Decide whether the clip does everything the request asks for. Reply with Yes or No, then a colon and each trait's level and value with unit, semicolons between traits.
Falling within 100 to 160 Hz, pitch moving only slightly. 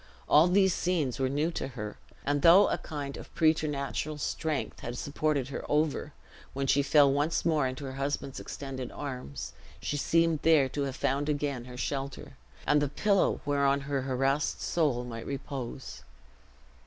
Yes: medium, 140 Hz; narrow, 2.3 semitones